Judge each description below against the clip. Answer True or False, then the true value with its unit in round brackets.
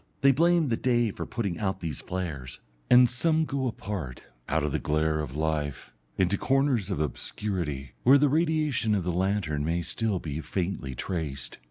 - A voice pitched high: False (95 Hz)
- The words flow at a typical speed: True (175 wpm)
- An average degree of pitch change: False (8.2 semitones)